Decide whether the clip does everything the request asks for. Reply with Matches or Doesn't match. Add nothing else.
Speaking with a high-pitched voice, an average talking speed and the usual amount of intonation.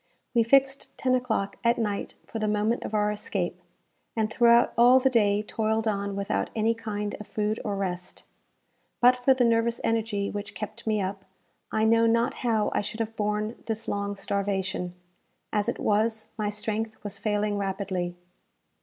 Doesn't match